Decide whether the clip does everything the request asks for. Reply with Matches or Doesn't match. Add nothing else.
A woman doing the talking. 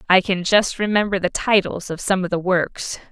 Matches